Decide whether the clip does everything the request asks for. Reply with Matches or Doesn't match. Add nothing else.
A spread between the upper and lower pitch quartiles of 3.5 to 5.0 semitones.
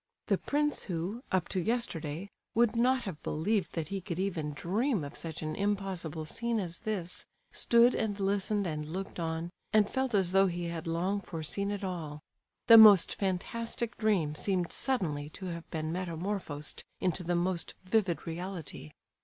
Matches